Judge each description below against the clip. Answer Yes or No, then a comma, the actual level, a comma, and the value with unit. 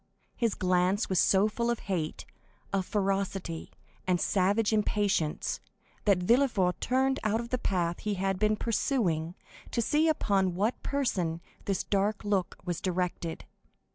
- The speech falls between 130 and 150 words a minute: Yes, average, 140 wpm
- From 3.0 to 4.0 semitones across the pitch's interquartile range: Yes, average, 3.6 semitones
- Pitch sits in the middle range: No, high, 195 Hz